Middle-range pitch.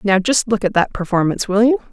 No: high, 210 Hz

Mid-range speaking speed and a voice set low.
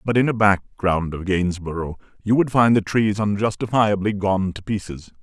Yes: average, 170 wpm; low, 100 Hz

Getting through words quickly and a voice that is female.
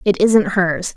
No: average, 190 wpm; female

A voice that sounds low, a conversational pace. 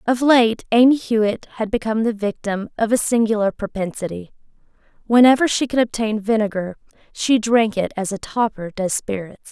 No: high, 220 Hz; average, 160 wpm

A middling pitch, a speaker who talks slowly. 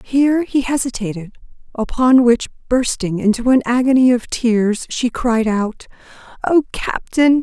No: high, 245 Hz; slow, 130 wpm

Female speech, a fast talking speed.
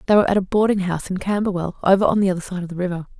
Yes: female; fast, 300 wpm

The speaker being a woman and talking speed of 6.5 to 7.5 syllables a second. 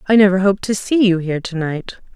Yes: female; 6.6 syllables/s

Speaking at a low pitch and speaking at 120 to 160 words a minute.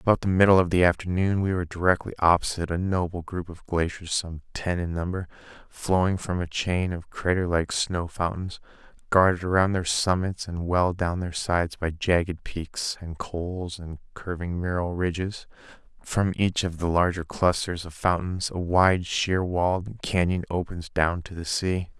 No: very low, 90 Hz; average, 175 wpm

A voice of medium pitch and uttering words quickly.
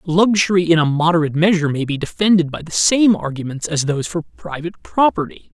No: medium, 165 Hz; average, 180 wpm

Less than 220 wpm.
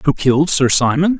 Yes: average, 200 wpm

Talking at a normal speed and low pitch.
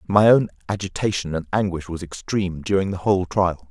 Yes: average, 180 wpm; very low, 95 Hz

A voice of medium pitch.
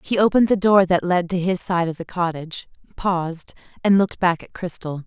Yes: medium, 180 Hz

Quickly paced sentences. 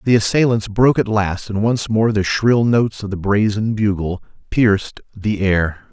No: average, 180 wpm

